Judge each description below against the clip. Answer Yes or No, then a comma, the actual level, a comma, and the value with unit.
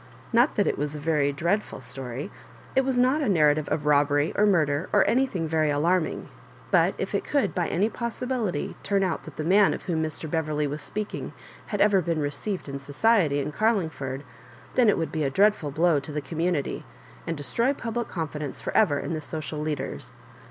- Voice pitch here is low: No, medium, 160 Hz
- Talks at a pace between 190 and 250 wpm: Yes, average, 195 wpm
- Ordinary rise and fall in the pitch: No, wide, 5.8 semitones